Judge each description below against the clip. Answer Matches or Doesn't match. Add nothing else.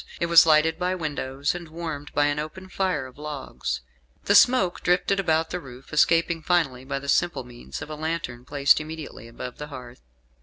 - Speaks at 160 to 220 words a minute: Matches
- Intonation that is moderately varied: Matches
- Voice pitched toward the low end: Doesn't match